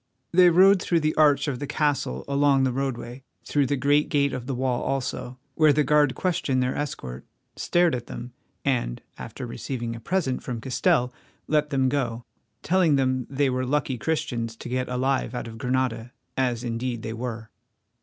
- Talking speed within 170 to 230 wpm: Yes, average, 180 wpm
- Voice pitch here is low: Yes, low, 130 Hz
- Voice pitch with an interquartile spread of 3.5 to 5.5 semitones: No, average, 3.1 semitones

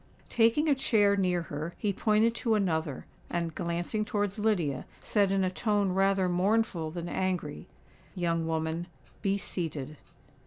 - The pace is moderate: Yes, average, 145 wpm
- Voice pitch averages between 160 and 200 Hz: Yes, medium, 185 Hz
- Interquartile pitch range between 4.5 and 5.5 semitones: No, average, 3.8 semitones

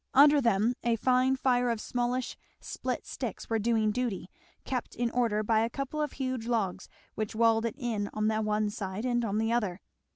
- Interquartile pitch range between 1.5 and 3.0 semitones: Yes, narrow, 2.6 semitones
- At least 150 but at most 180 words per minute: No, average, 195 wpm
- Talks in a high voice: Yes, high, 230 Hz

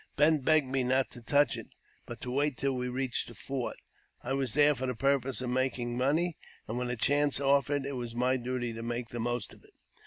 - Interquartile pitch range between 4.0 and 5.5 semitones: No, narrow, 2.4 semitones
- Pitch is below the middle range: Yes, low, 130 Hz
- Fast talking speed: Yes, fast, 230 wpm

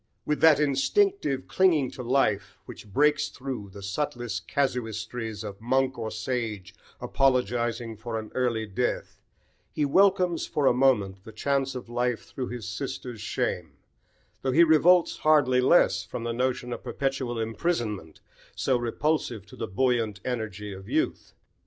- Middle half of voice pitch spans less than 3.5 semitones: No, average, 3.8 semitones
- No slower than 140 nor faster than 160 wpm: Yes, average, 145 wpm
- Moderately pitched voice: No, low, 125 Hz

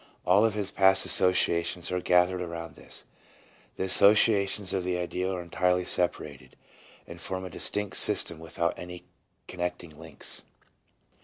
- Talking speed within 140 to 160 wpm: Yes, average, 145 wpm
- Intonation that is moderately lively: No, narrow, 1.6 semitones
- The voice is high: No, very low, 90 Hz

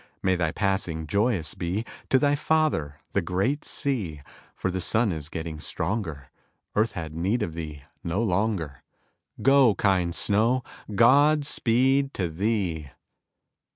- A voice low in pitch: Yes, low, 100 Hz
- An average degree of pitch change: No, wide, 6.6 semitones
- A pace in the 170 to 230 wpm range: No, slow, 135 wpm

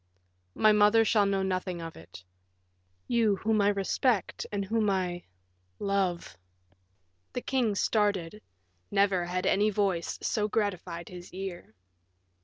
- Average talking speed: No, slow, 130 wpm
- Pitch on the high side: Yes, high, 195 Hz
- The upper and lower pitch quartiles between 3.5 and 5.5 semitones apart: No, average, 3.0 semitones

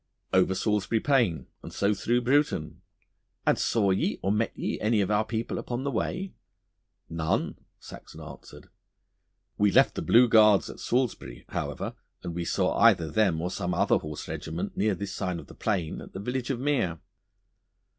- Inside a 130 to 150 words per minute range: No, average, 175 wpm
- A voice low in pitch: Yes, low, 105 Hz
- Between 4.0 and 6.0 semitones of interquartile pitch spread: Yes, average, 4.9 semitones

